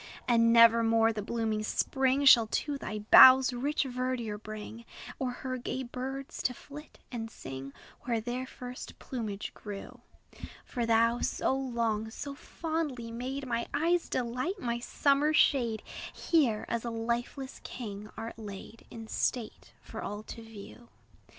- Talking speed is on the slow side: No, average, 145 wpm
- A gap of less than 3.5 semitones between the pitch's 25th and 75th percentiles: Yes, average, 2.7 semitones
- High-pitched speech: Yes, high, 235 Hz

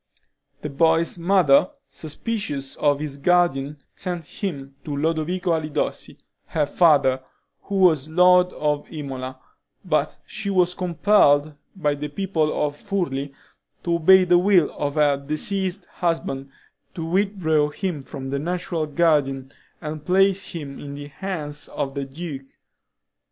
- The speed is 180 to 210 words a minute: No, slow, 135 wpm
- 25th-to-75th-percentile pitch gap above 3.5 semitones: Yes, average, 3.9 semitones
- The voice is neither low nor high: Yes, medium, 155 Hz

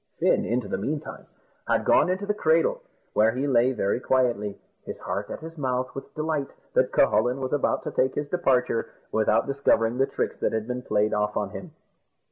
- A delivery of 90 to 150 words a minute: No, average, 195 wpm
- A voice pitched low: Yes, low, 130 Hz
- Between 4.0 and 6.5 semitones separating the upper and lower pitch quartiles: Yes, average, 4.5 semitones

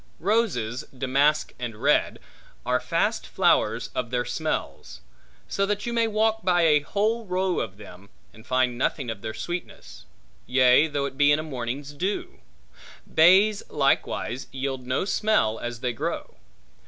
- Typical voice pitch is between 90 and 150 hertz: Yes, medium, 140 Hz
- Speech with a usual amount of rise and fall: No, wide, 7.3 semitones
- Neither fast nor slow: Yes, average, 155 wpm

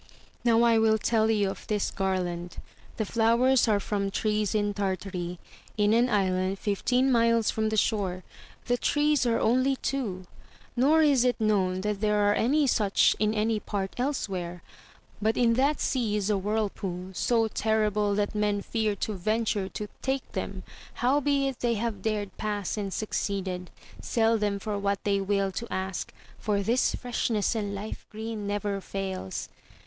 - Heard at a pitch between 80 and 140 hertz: No, high, 210 Hz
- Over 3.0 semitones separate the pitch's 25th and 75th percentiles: No, narrow, 2.6 semitones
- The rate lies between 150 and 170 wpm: Yes, average, 165 wpm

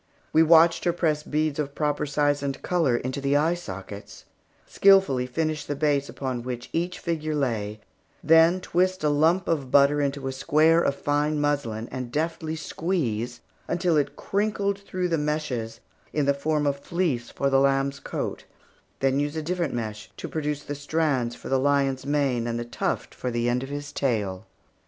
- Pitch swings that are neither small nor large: Yes, average, 3.5 semitones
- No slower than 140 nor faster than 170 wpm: No, average, 180 wpm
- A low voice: No, medium, 145 Hz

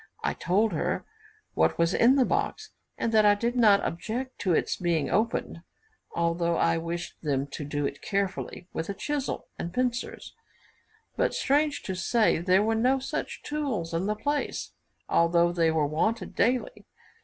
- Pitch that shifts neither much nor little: No, wide, 6.2 semitones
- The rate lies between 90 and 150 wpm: No, average, 165 wpm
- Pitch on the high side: Yes, high, 200 Hz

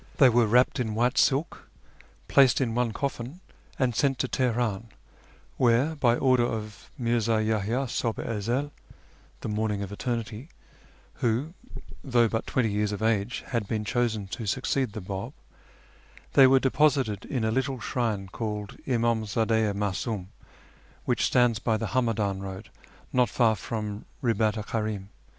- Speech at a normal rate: Yes, average, 155 wpm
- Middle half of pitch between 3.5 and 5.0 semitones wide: No, average, 2.9 semitones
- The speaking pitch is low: Yes, low, 115 Hz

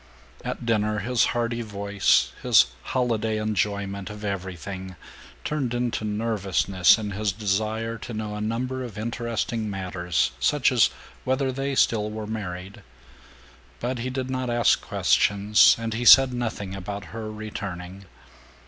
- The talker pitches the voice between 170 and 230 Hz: No, low, 110 Hz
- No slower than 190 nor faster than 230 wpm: No, average, 140 wpm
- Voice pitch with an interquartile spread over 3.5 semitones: No, average, 2.9 semitones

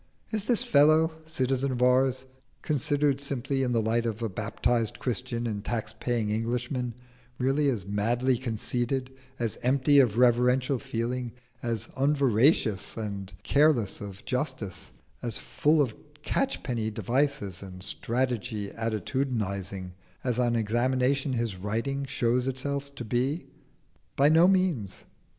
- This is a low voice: Yes, low, 125 Hz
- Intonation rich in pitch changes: No, average, 3.5 semitones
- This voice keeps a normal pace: No, slow, 130 wpm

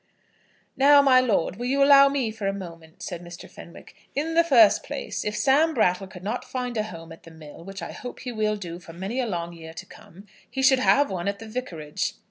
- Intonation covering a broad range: Yes, wide, 6.9 semitones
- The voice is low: No, high, 210 Hz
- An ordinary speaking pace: No, fast, 235 wpm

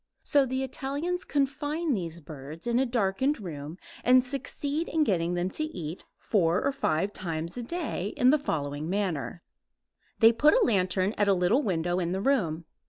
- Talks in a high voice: Yes, high, 200 Hz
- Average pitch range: No, wide, 8.1 semitones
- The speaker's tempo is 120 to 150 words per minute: No, average, 175 wpm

